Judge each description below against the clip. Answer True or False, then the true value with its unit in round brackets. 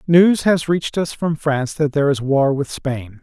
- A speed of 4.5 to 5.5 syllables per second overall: True (4.9 syllables/s)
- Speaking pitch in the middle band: True (145 Hz)